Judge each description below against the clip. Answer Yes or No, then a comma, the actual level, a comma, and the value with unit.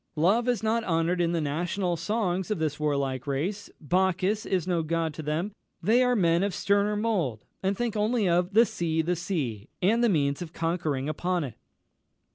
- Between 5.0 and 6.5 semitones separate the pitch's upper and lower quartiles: No, average, 4.3 semitones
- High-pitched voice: No, medium, 175 Hz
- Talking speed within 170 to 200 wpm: Yes, average, 190 wpm